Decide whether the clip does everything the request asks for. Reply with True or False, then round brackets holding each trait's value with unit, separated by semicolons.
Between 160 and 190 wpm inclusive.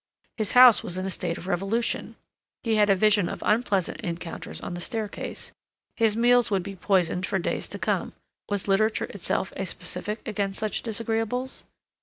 True (175 wpm)